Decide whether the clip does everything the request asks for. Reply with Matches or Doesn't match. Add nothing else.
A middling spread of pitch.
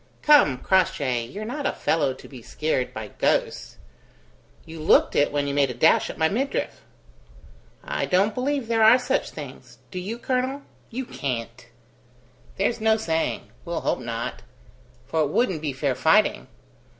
Doesn't match